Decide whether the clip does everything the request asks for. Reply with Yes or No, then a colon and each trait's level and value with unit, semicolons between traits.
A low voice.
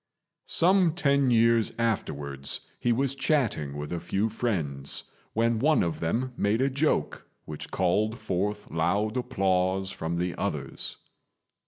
Yes: low, 105 Hz